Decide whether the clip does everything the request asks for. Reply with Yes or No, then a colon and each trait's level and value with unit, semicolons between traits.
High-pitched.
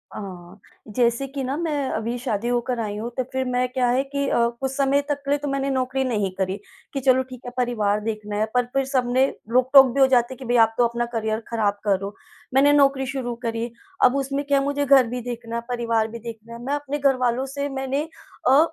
Yes: very high, 250 Hz